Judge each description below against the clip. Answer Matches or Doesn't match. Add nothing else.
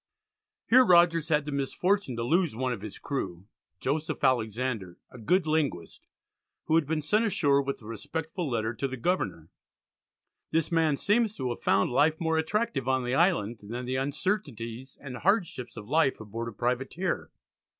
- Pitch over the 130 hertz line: Matches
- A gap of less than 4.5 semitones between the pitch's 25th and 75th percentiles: Doesn't match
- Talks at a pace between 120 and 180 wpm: Matches